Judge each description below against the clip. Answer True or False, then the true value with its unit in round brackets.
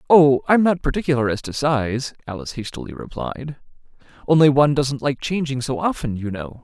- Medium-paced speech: True (170 wpm)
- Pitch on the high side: False (135 Hz)